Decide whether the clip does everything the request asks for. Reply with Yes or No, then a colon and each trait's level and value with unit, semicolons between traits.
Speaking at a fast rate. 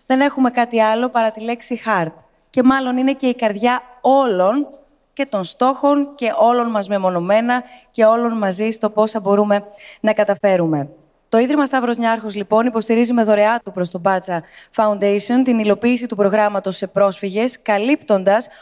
No: average, 160 wpm